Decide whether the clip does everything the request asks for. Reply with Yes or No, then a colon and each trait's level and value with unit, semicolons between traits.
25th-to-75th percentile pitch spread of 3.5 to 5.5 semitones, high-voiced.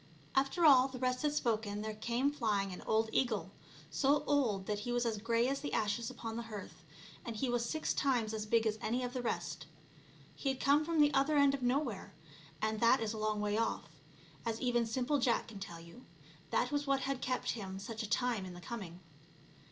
Yes: average, 3.8 semitones; high, 235 Hz